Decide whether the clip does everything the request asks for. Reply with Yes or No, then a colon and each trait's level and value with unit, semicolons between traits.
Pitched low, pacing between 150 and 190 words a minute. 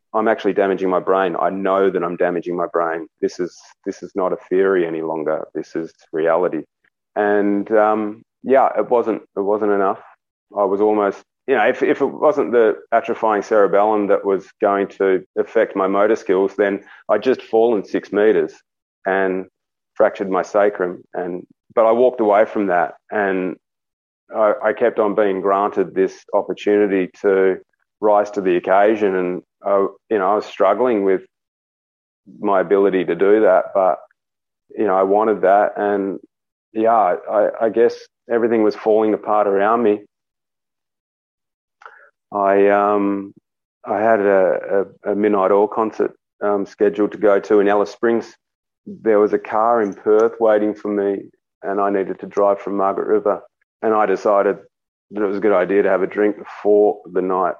Yes: low, 100 Hz; average, 170 wpm